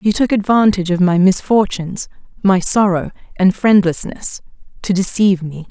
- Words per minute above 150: No, slow, 135 wpm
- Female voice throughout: Yes, female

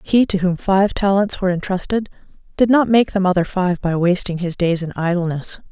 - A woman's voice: Yes, female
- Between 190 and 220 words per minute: Yes, average, 200 wpm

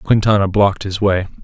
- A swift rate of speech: No, average, 165 wpm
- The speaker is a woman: No, male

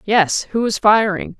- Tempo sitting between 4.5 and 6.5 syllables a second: No, 4.1 syllables/s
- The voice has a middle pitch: No, high, 205 Hz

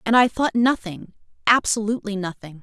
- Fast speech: No, slow, 135 wpm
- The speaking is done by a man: No, female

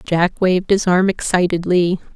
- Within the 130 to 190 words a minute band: Yes, average, 140 wpm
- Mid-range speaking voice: Yes, medium, 180 Hz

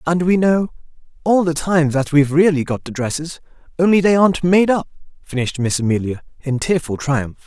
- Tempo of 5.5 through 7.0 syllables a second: Yes, 5.6 syllables/s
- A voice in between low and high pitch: Yes, medium, 160 Hz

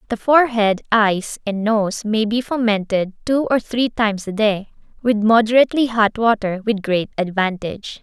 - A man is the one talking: No, female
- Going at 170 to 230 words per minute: No, average, 155 wpm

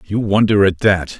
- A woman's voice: No, male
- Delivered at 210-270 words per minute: No, average, 200 wpm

